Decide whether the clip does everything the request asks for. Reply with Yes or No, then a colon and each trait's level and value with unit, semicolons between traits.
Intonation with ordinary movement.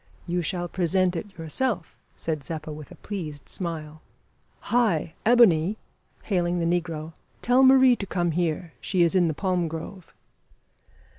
Yes: average, 3.1 semitones